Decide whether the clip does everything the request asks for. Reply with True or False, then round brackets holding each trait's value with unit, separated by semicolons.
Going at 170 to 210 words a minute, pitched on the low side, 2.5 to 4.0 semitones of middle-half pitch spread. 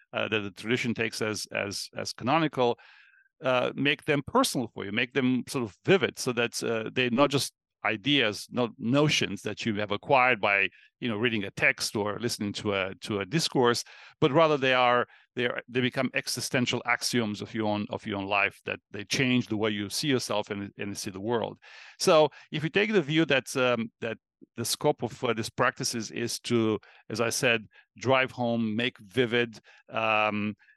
True (200 wpm; 120 Hz; 3.7 semitones)